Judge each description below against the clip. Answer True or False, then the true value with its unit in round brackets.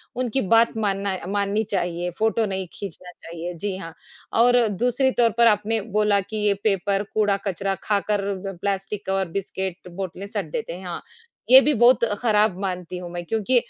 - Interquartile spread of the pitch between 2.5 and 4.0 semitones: True (2.8 semitones)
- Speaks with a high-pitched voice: True (200 Hz)